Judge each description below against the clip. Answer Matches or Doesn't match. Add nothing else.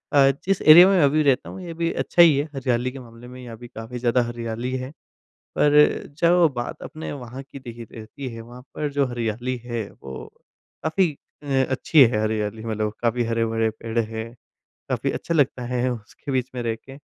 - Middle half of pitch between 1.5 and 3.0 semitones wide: Doesn't match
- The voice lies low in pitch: Matches